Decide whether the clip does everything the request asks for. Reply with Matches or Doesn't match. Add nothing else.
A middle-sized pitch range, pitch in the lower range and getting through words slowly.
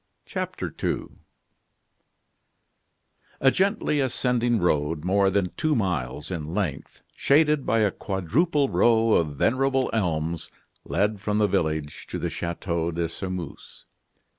Doesn't match